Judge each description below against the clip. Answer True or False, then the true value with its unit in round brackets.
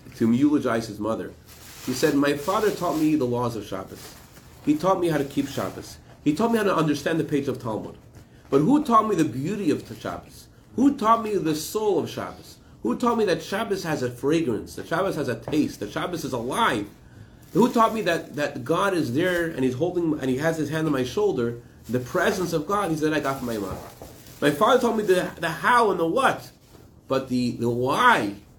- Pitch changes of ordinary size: False (7.6 semitones)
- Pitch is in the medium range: True (155 Hz)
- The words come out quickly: True (225 wpm)